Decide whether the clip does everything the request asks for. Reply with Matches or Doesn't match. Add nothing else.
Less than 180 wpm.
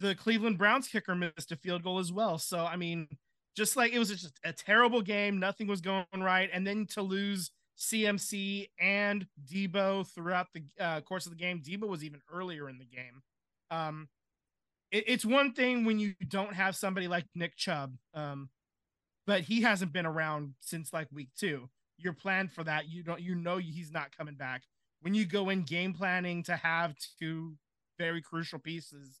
Doesn't match